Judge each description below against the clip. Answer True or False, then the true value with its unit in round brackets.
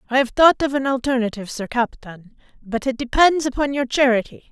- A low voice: False (255 Hz)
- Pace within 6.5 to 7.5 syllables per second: False (5.7 syllables/s)